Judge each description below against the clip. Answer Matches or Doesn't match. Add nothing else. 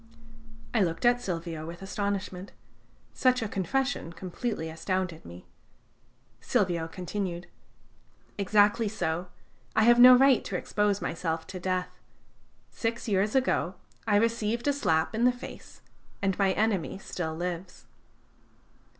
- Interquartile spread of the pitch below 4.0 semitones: Doesn't match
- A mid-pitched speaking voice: Doesn't match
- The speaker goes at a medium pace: Doesn't match